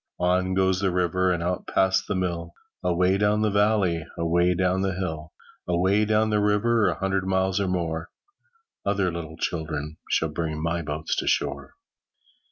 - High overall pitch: No, very low, 90 Hz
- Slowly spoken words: No, average, 165 wpm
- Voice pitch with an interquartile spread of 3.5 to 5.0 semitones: No, narrow, 2.4 semitones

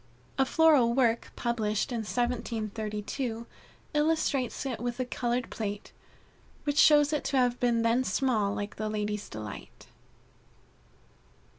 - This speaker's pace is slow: Yes, slow, 125 wpm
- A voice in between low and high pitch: No, high, 235 Hz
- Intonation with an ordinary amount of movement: Yes, average, 3.4 semitones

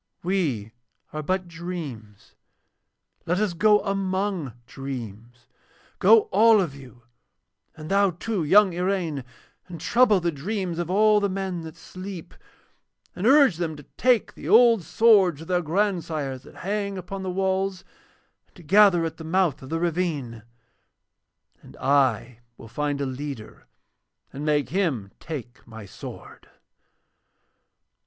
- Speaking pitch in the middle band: Yes, medium, 175 Hz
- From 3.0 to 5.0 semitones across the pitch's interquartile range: No, wide, 5.5 semitones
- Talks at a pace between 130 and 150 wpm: Yes, average, 140 wpm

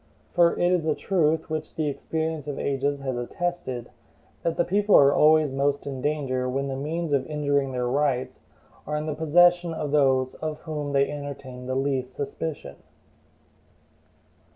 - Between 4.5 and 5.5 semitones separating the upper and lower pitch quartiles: No, average, 2.8 semitones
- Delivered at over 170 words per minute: No, average, 165 wpm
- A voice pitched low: No, medium, 145 Hz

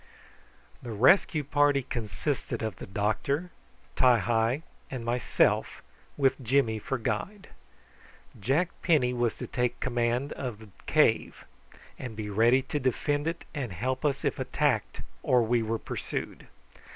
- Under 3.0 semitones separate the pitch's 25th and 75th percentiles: No, average, 3.8 semitones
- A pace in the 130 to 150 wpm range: Yes, average, 140 wpm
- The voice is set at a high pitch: No, low, 125 Hz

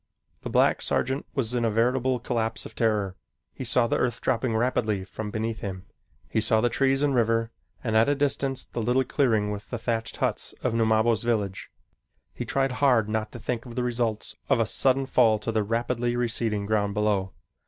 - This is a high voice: No, low, 115 Hz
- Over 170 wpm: Yes, average, 195 wpm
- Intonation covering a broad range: No, narrow, 2.4 semitones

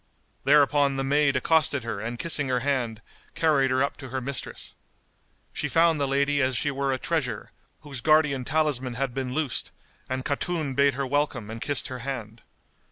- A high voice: No, low, 135 Hz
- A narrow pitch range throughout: Yes, narrow, 2.2 semitones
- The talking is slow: No, average, 180 wpm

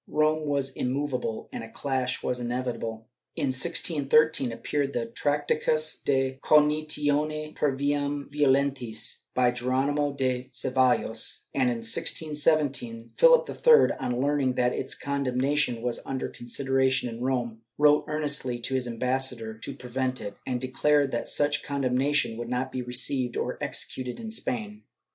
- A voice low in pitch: Yes, low, 130 Hz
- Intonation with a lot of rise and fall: No, average, 2.9 semitones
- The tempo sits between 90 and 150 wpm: Yes, average, 140 wpm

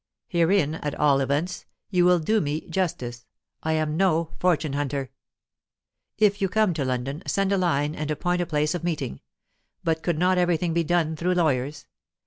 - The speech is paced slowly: No, average, 175 wpm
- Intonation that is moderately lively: Yes, average, 3.3 semitones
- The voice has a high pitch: No, medium, 160 Hz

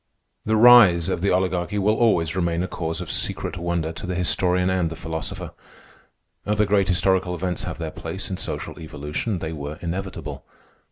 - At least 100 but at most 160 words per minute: No, average, 175 wpm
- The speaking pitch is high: No, very low, 90 Hz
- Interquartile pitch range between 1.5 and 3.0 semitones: Yes, narrow, 2.6 semitones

